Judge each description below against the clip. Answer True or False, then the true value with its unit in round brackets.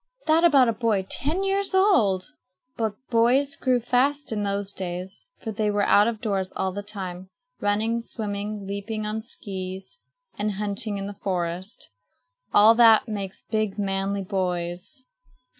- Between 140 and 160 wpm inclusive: True (150 wpm)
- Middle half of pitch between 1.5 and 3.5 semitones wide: True (3.1 semitones)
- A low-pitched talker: False (210 Hz)